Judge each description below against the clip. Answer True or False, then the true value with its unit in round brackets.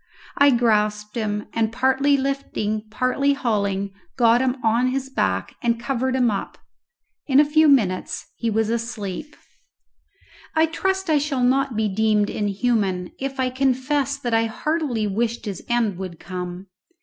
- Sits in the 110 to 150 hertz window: False (235 Hz)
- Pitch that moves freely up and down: False (4.4 semitones)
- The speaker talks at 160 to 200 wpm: False (150 wpm)